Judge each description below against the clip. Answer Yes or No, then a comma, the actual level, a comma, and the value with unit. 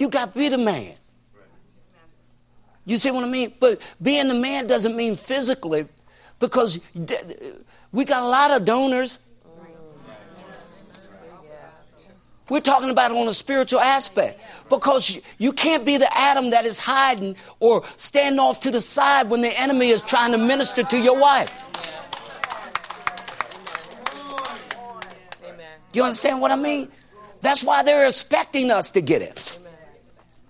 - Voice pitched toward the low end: No, very high, 255 Hz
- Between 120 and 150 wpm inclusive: Yes, average, 140 wpm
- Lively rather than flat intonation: No, average, 4.3 semitones